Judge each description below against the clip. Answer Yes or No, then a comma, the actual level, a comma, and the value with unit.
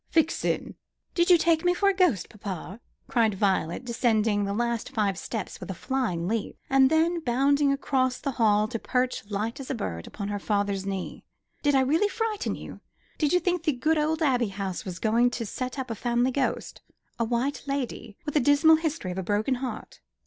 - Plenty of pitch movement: Yes, wide, 5.9 semitones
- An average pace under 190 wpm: No, average, 200 wpm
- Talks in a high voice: Yes, high, 245 Hz